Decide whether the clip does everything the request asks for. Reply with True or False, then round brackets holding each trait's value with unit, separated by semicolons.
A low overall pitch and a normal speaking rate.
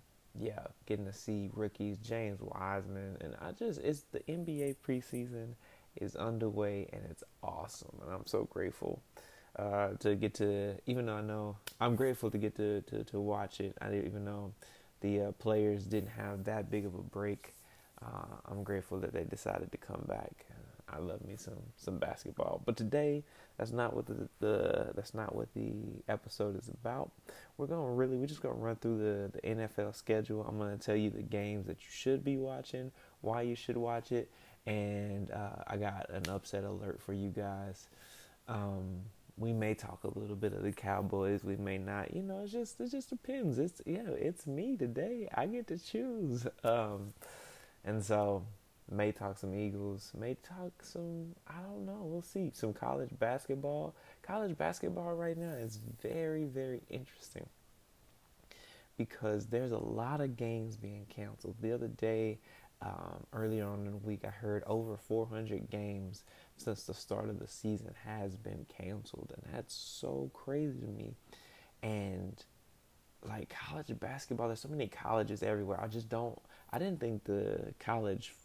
True (110 Hz; 180 wpm)